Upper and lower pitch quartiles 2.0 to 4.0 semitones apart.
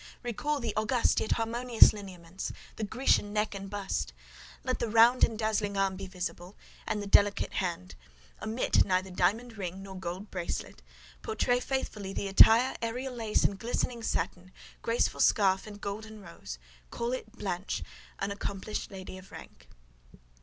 Yes: average, 3.1 semitones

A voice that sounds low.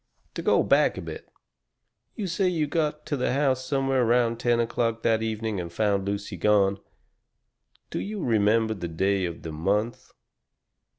Yes: low, 115 Hz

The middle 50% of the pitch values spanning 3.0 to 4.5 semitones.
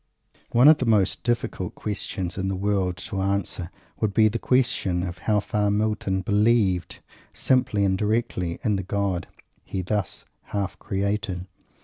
No: narrow, 2.4 semitones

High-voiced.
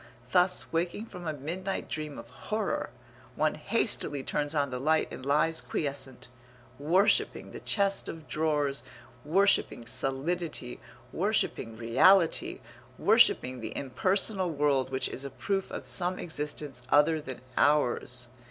No: medium, 150 Hz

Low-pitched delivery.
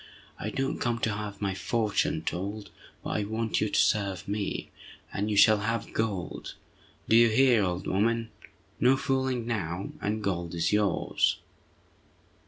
Yes: low, 105 Hz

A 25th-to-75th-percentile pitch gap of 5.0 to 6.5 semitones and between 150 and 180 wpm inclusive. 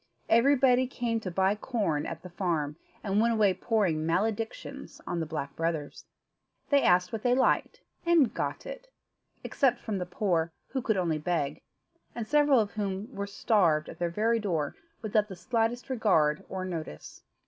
Yes: wide, 5.5 semitones; average, 170 wpm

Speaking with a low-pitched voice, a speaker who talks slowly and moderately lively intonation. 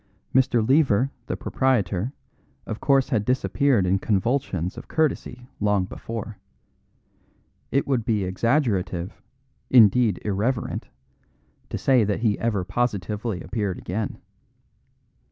Yes: low, 110 Hz; slow, 110 wpm; average, 4.5 semitones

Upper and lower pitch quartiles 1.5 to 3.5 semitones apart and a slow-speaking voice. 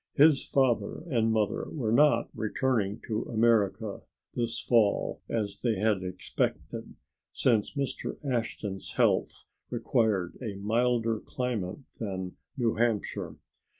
Yes: average, 3.0 semitones; slow, 115 wpm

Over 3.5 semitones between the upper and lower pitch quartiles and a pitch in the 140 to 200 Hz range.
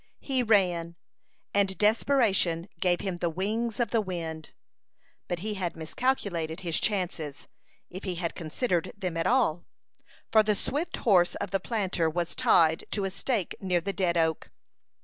Yes: average, 4.0 semitones; medium, 185 Hz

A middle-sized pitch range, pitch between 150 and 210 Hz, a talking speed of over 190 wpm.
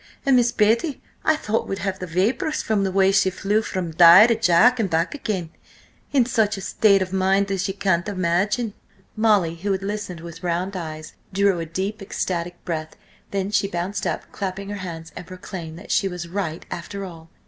Yes: average, 3.0 semitones; high, 190 Hz; average, 200 wpm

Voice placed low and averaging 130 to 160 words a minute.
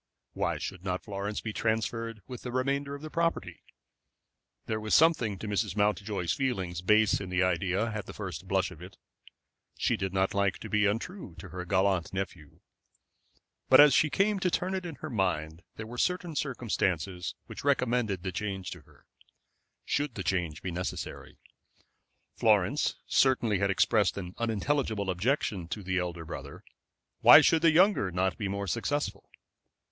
No: low, 105 Hz; average, 170 wpm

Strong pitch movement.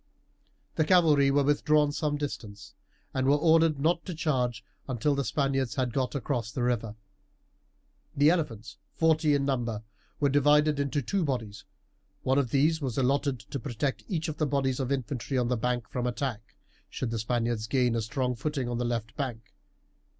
No: average, 3.4 semitones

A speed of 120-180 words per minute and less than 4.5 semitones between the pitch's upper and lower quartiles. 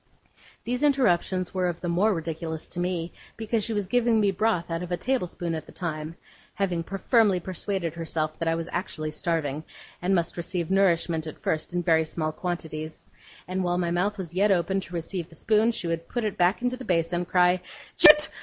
No: fast, 205 wpm; average, 2.9 semitones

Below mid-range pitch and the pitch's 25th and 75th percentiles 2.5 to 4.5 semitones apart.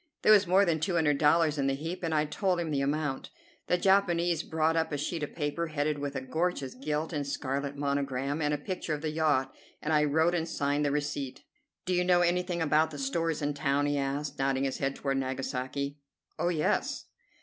No: medium, 150 Hz; average, 2.9 semitones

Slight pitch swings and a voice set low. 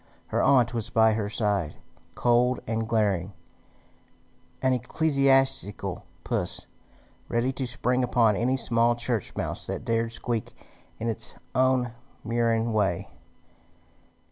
Yes: narrow, 2.2 semitones; low, 115 Hz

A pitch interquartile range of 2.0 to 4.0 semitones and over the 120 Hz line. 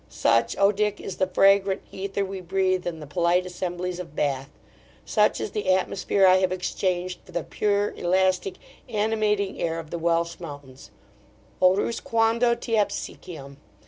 Yes: average, 2.7 semitones; medium, 185 Hz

